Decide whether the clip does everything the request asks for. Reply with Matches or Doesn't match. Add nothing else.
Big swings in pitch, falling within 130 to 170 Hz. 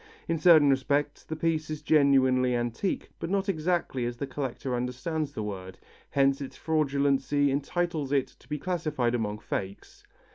Doesn't match